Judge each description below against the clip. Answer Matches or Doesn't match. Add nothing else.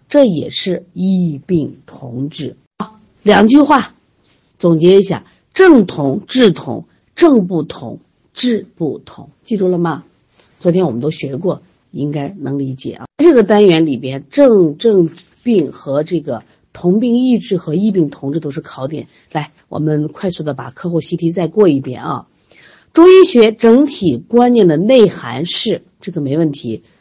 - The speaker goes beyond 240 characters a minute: Doesn't match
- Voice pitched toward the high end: Doesn't match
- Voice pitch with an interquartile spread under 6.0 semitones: Doesn't match